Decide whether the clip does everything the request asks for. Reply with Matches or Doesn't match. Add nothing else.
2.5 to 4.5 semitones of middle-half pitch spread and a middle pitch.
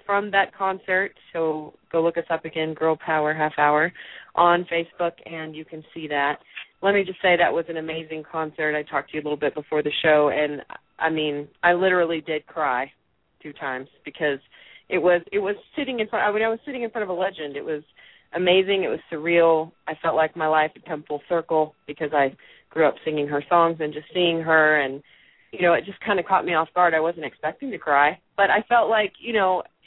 Matches